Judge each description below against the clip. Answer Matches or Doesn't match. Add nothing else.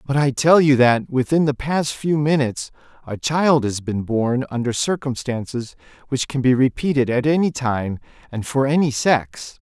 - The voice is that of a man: Matches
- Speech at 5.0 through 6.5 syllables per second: Doesn't match